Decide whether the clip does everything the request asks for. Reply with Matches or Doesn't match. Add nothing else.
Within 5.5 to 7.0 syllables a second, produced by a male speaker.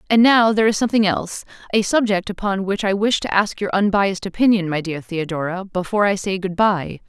Doesn't match